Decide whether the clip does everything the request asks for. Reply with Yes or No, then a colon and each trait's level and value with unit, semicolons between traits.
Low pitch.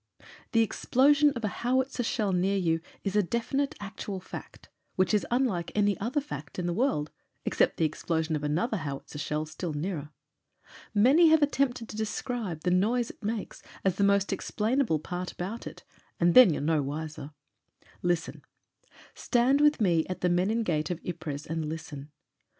No: high, 190 Hz